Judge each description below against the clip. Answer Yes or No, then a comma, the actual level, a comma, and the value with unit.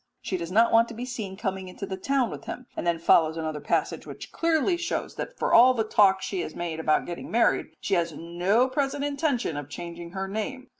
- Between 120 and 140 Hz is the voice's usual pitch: No, high, 195 Hz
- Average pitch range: No, wide, 6.6 semitones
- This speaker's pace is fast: Yes, fast, 230 wpm